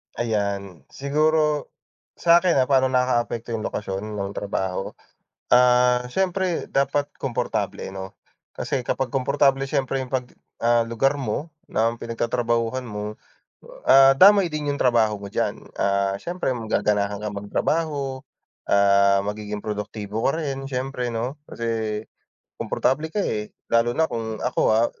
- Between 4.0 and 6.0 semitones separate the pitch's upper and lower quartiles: Yes, average, 4.4 semitones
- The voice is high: No, low, 120 Hz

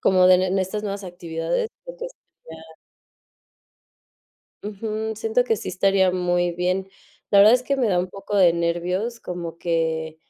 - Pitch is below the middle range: No, medium, 185 Hz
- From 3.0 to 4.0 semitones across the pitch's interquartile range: Yes, average, 3.5 semitones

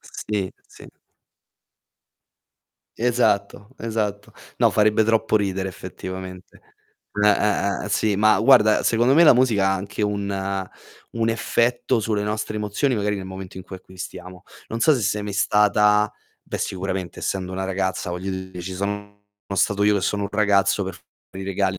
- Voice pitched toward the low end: Yes, low, 100 Hz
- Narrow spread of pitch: Yes, narrow, 2.0 semitones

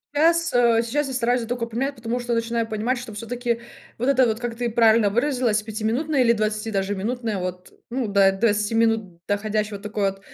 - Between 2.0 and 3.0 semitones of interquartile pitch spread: Yes, narrow, 2.5 semitones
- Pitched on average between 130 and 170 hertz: No, high, 230 Hz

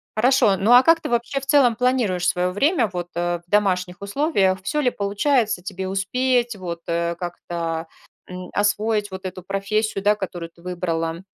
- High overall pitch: Yes, high, 195 Hz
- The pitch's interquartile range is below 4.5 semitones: No, average, 4.8 semitones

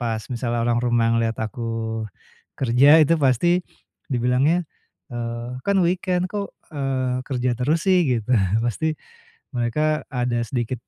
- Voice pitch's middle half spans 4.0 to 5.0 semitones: Yes, average, 4.4 semitones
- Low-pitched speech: Yes, low, 125 Hz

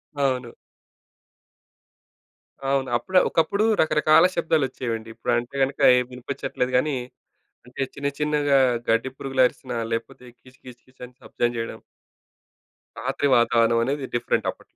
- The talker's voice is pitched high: No, low, 130 Hz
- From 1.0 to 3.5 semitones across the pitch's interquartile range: Yes, average, 2.9 semitones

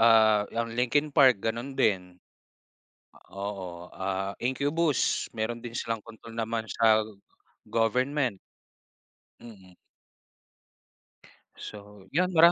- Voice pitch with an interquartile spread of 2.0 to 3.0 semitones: No, average, 3.6 semitones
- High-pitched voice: No, low, 115 Hz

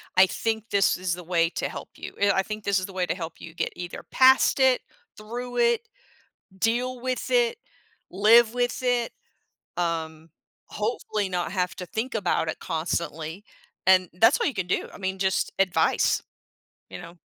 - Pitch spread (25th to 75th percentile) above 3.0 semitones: Yes, average, 5.0 semitones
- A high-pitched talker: Yes, high, 195 Hz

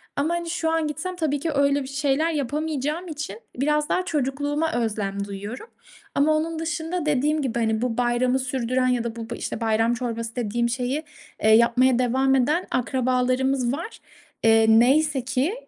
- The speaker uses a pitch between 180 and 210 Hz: No, very high, 265 Hz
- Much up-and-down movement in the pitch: No, average, 4.2 semitones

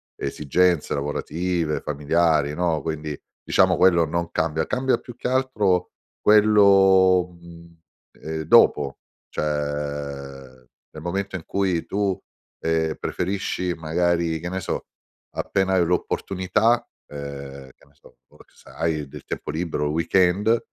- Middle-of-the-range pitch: No, very low, 85 Hz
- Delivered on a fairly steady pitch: No, average, 3.9 semitones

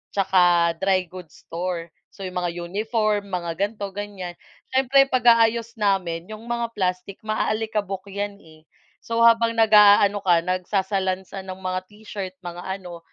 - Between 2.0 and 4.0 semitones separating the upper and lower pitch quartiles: Yes, average, 2.9 semitones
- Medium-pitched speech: No, high, 195 Hz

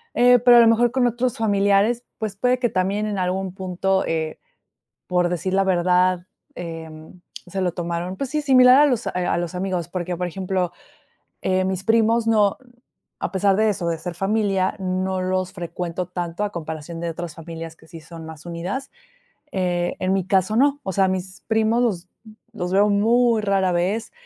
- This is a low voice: No, high, 190 Hz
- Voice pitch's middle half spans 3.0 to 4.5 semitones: Yes, average, 3.6 semitones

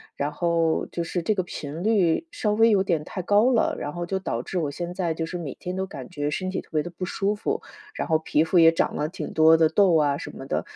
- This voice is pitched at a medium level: Yes, medium, 175 Hz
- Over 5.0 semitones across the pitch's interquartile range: No, average, 3.1 semitones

